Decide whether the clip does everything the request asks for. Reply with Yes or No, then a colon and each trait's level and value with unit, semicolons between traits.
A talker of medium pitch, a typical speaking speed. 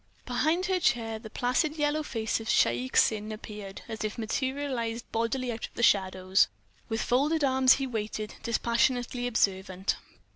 No: high, 230 Hz; average, 150 wpm